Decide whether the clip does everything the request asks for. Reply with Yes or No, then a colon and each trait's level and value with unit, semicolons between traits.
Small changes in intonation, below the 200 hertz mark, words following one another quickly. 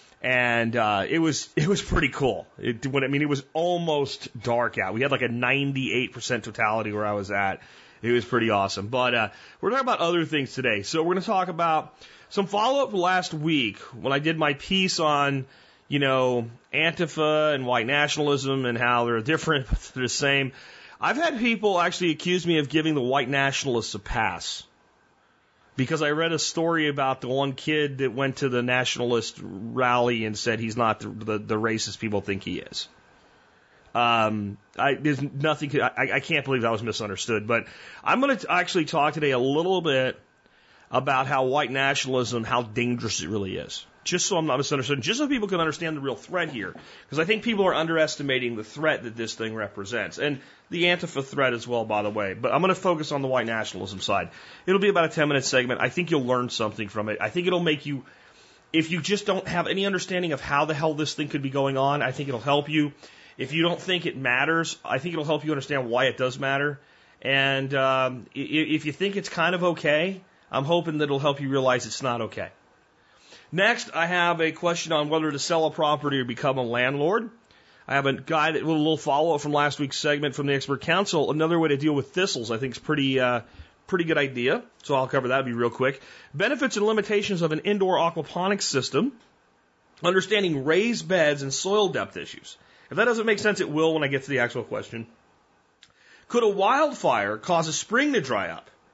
No: average, 4.8 semitones; medium, 140 Hz; fast, 215 wpm